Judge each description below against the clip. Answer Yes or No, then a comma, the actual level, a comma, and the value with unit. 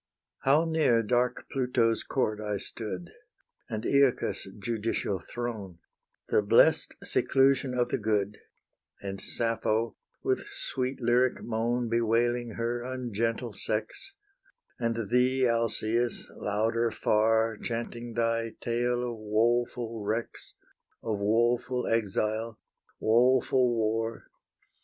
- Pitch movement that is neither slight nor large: No, narrow, 1.9 semitones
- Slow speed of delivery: Yes, slow, 105 wpm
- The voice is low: Yes, low, 115 Hz